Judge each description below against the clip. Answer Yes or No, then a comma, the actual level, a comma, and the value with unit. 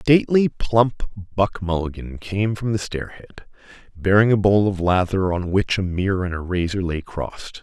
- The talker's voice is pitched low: Yes, very low, 95 Hz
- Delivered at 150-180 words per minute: Yes, average, 175 wpm